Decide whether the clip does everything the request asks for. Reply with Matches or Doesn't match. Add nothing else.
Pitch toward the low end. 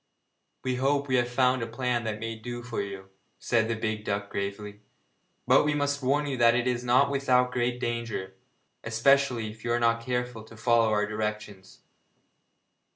Matches